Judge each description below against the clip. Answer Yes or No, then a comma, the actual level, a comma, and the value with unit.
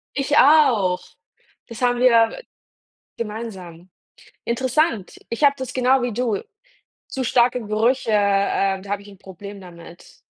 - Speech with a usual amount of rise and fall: Yes, average, 4.3 semitones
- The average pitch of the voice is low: No, high, 225 Hz